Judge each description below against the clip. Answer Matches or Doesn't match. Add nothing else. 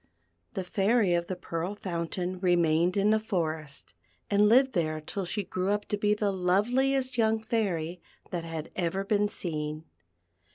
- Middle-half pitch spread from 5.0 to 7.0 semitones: Doesn't match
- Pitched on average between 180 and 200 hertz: Matches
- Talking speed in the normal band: Matches